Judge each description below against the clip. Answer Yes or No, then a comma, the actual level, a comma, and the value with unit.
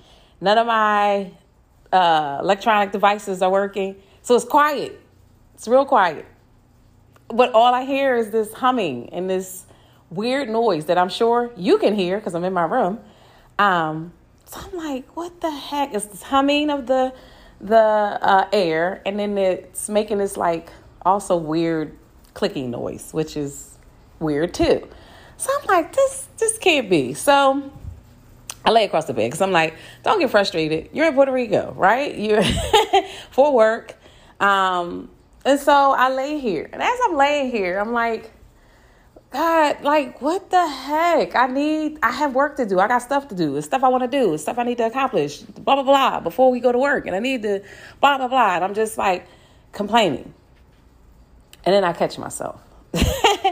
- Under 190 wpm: Yes, average, 180 wpm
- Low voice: No, high, 225 Hz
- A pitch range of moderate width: No, wide, 6.6 semitones